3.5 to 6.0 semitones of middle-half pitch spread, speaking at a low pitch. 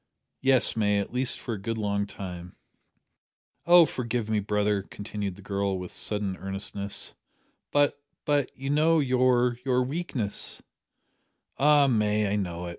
Yes: average, 4.5 semitones; low, 105 Hz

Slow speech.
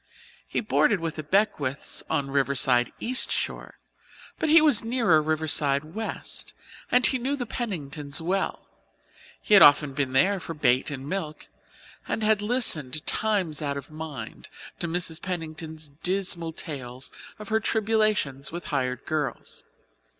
No: average, 145 wpm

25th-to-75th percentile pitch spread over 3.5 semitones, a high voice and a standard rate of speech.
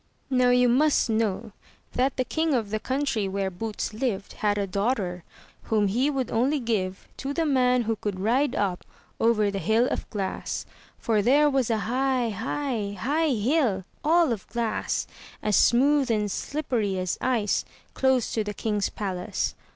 Yes: average, 4.3 semitones; high, 230 Hz; average, 165 wpm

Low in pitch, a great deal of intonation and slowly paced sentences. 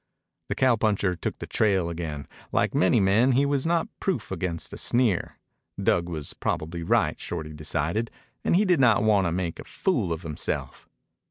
No: very low, 95 Hz; wide, 6.4 semitones; average, 175 wpm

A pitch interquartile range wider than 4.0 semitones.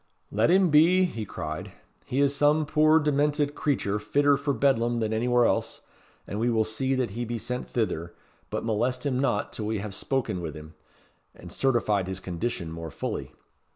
Yes: wide, 5.4 semitones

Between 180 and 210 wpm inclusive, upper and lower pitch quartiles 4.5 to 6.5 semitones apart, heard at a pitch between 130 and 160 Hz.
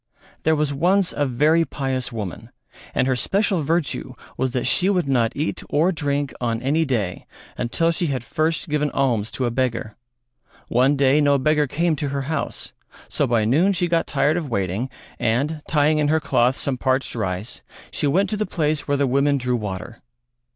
No: average, 190 wpm; average, 4.0 semitones; medium, 140 Hz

